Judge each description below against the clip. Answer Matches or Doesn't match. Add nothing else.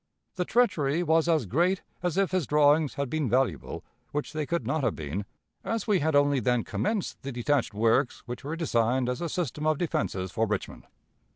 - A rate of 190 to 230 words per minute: Matches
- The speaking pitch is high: Doesn't match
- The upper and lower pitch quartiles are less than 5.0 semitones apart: Doesn't match